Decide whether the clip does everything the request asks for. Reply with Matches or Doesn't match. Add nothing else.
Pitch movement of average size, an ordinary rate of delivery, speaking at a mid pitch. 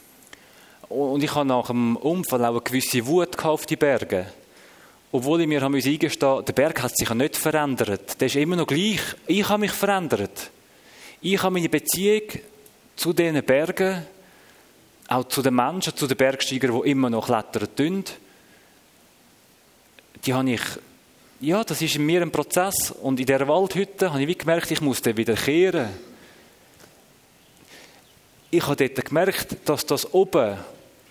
Matches